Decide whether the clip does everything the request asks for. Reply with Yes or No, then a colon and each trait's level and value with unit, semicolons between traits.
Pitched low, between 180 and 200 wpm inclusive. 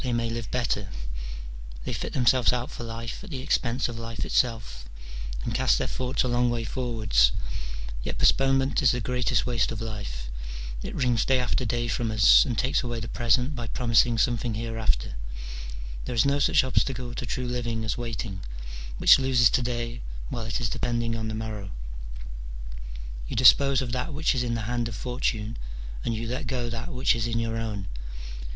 Yes: low, 120 Hz; average, 190 wpm